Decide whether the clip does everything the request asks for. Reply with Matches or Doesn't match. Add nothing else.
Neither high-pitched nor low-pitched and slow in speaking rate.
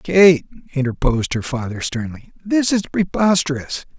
Matches